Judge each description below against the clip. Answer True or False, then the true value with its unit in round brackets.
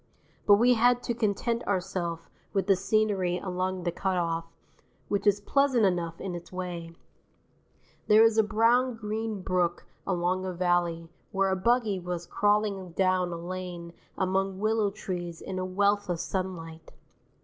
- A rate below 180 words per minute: True (155 wpm)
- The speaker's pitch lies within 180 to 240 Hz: True (190 Hz)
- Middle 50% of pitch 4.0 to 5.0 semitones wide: False (2.9 semitones)